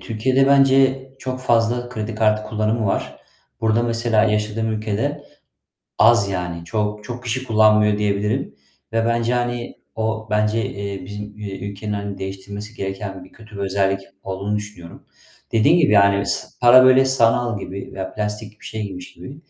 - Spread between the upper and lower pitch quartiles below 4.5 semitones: Yes, average, 2.8 semitones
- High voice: No, low, 110 Hz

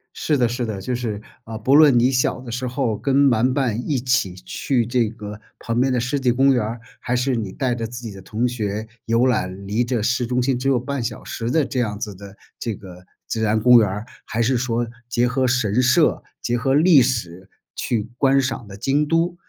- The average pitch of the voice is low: Yes, low, 120 Hz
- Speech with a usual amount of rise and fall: Yes, average, 3.0 semitones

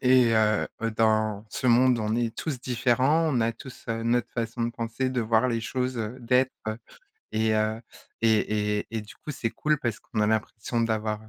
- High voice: No, low, 115 Hz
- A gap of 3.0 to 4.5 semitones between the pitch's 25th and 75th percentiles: No, narrow, 2.4 semitones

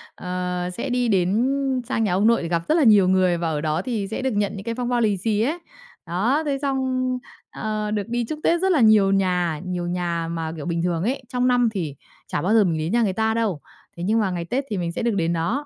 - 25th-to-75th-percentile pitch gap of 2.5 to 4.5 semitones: No, average, 5.2 semitones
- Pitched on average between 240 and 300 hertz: No, high, 205 Hz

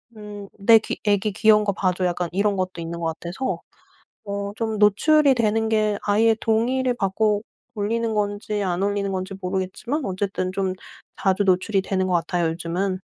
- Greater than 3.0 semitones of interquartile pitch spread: No, narrow, 2.6 semitones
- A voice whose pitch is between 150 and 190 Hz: No, high, 200 Hz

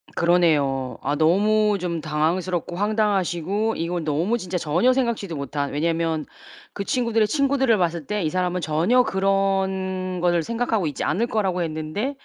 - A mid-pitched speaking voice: Yes, medium, 180 Hz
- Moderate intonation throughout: Yes, average, 4.5 semitones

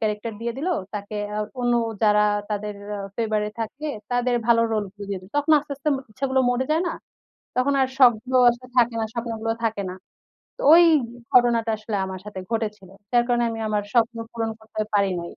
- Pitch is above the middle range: Yes, high, 225 Hz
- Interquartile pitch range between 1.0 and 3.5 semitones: Yes, narrow, 2.6 semitones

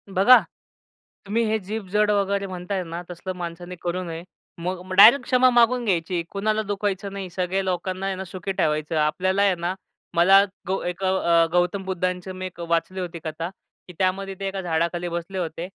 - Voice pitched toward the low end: No, medium, 185 Hz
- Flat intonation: Yes, narrow, 2.1 semitones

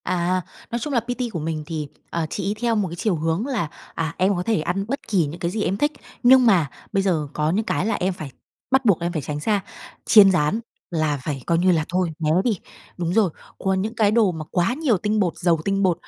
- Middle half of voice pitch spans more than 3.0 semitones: Yes, average, 4.7 semitones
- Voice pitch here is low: No, medium, 185 Hz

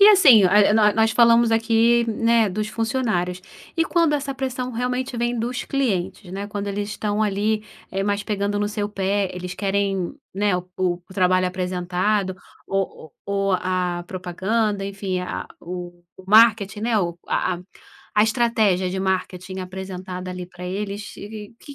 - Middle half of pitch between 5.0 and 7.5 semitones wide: No, average, 3.3 semitones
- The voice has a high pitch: Yes, high, 205 Hz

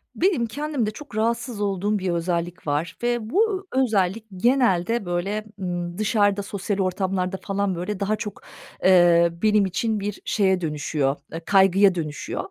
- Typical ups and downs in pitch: Yes, average, 3.6 semitones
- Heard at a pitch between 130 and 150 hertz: No, high, 195 Hz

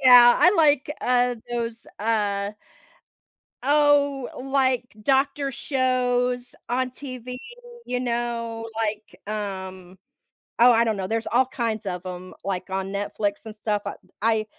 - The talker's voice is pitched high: Yes, high, 235 Hz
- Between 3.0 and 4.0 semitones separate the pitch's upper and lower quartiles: Yes, average, 3.5 semitones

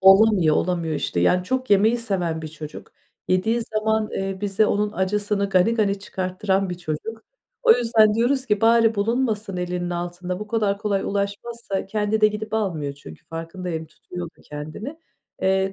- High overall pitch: Yes, high, 200 Hz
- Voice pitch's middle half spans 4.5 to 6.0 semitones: No, average, 3.4 semitones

